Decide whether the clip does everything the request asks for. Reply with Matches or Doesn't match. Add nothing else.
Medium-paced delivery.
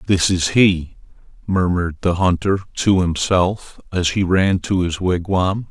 Matches